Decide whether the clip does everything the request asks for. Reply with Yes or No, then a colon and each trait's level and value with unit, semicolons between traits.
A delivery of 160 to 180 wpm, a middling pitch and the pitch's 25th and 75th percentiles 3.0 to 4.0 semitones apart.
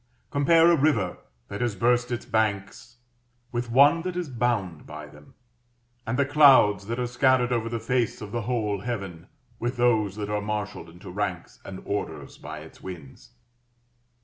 No: average, 170 wpm; low, 115 Hz; average, 3.7 semitones